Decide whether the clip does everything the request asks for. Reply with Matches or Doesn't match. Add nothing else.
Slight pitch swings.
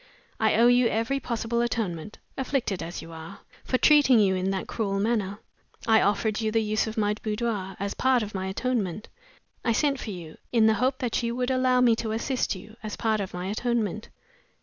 Doesn't match